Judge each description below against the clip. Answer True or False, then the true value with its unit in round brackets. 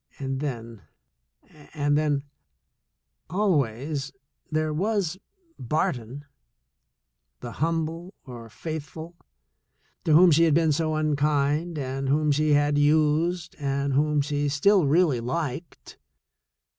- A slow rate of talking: True (120 wpm)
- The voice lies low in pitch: False (150 Hz)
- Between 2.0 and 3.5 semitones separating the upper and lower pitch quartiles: True (2.6 semitones)